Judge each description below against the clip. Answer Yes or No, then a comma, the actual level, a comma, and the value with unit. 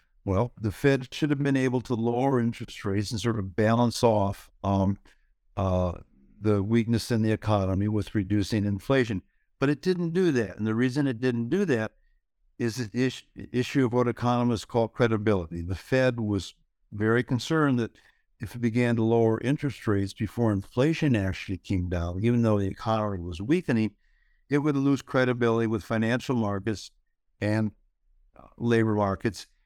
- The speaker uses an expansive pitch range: No, average, 3.7 semitones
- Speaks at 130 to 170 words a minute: Yes, average, 165 wpm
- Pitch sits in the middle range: No, low, 115 Hz